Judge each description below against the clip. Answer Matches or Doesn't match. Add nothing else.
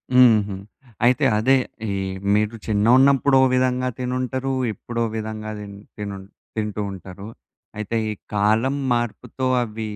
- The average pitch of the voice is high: Doesn't match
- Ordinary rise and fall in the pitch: Matches